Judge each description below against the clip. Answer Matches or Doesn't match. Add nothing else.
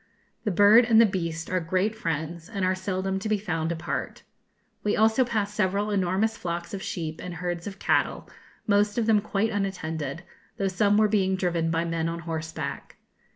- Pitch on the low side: Doesn't match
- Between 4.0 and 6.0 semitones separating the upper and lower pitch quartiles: Doesn't match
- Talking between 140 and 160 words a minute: Doesn't match